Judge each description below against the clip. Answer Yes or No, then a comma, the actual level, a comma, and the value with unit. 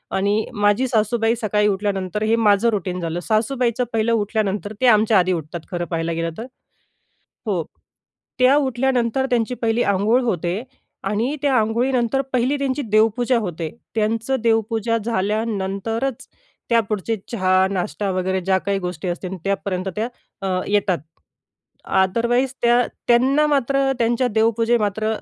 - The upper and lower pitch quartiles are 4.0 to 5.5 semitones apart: No, average, 3.6 semitones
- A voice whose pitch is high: Yes, high, 220 Hz